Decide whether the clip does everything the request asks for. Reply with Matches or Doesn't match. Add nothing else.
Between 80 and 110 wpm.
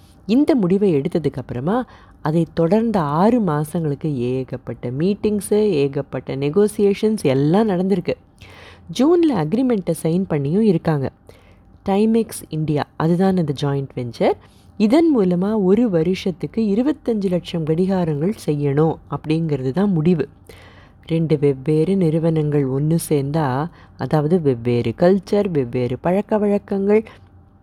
Matches